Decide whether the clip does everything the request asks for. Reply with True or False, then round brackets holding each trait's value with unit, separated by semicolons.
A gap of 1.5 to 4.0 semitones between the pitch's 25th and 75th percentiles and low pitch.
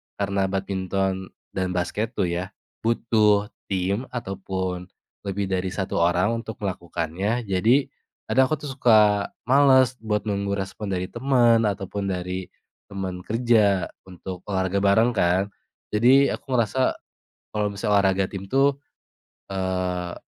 True (3.3 semitones; 100 Hz)